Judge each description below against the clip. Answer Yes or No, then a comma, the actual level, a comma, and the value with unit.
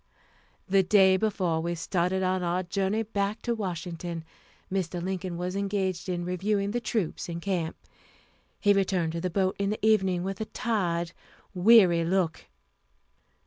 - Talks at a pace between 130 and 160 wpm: Yes, average, 150 wpm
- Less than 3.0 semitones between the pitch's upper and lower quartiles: Yes, narrow, 2.4 semitones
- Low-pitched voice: No, medium, 185 Hz